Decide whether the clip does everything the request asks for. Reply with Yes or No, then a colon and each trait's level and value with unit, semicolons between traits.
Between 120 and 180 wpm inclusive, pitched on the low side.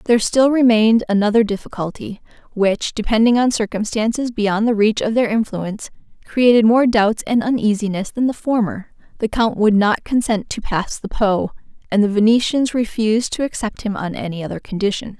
No: average, 170 wpm; high, 220 Hz